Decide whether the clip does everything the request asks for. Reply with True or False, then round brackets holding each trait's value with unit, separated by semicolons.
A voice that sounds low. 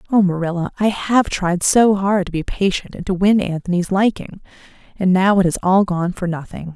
False (190 Hz)